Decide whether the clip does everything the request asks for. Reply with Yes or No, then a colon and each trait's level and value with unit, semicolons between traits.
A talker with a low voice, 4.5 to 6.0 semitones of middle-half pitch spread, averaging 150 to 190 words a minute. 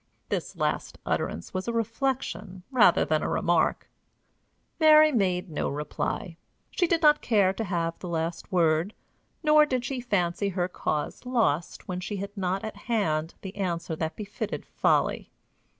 No: high, 195 Hz; wide, 5.4 semitones; average, 155 wpm